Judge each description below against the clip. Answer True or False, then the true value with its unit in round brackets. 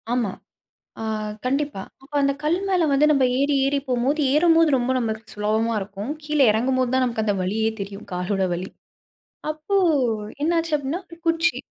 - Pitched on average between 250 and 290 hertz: True (260 Hz)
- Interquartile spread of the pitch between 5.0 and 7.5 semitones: True (5.6 semitones)